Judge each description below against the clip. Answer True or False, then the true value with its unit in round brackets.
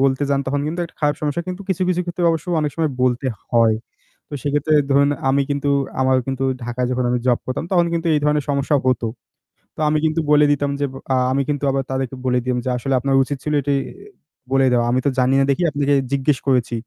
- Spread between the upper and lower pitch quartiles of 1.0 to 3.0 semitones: True (2.4 semitones)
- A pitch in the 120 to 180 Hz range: True (140 Hz)